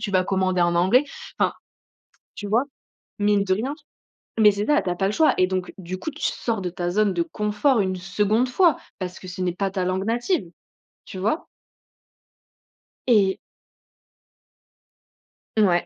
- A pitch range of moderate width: Yes, average, 3.0 semitones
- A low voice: No, high, 195 Hz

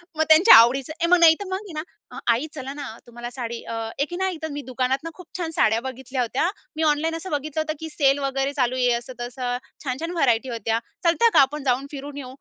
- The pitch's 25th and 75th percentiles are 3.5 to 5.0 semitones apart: Yes, average, 4.1 semitones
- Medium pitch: No, very high, 275 Hz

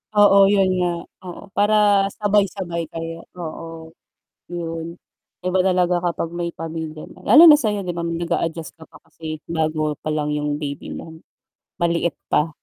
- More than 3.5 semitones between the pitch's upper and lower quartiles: No, average, 3.0 semitones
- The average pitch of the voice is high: No, medium, 170 Hz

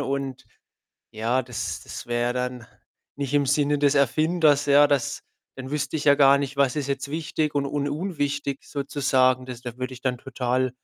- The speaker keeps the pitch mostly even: Yes, narrow, 2.1 semitones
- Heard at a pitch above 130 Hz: Yes, medium, 140 Hz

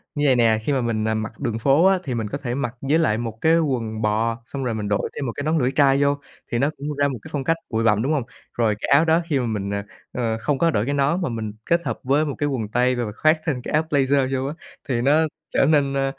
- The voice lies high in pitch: No, low, 135 Hz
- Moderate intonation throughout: Yes, average, 4.1 semitones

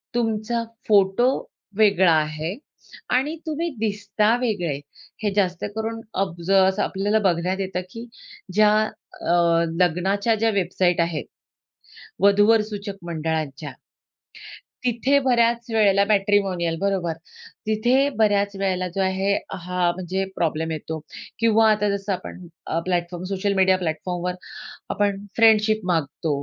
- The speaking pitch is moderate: No, high, 195 Hz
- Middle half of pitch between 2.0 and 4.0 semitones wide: Yes, average, 3.4 semitones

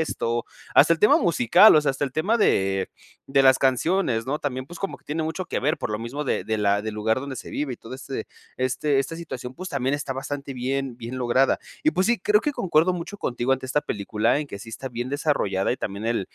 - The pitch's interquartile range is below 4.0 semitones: No, average, 4.7 semitones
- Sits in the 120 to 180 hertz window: Yes, low, 135 Hz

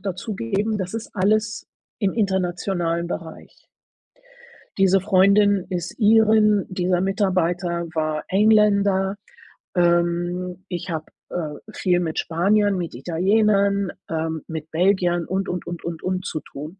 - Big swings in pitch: No, average, 2.7 semitones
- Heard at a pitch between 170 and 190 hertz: Yes, medium, 185 Hz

